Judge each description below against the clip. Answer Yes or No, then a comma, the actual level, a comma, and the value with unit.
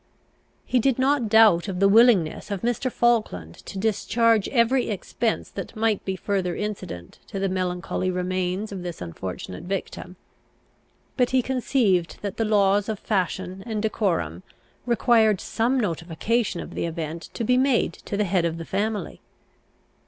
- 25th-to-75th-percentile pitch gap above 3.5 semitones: Yes, average, 4.2 semitones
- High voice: Yes, high, 200 Hz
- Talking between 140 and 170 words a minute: Yes, average, 155 wpm